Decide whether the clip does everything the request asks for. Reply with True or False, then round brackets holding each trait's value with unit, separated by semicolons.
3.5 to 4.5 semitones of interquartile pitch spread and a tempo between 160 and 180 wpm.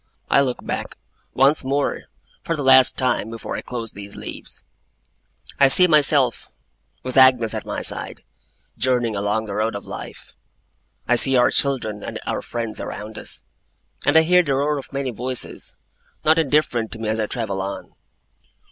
True (3.9 semitones; 170 wpm)